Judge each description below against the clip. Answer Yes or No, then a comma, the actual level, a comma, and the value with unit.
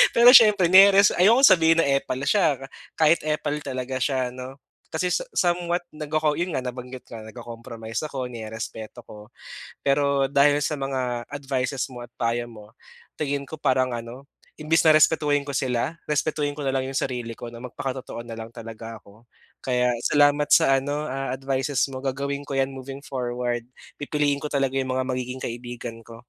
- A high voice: No, low, 135 Hz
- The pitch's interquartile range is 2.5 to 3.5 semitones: Yes, average, 3.2 semitones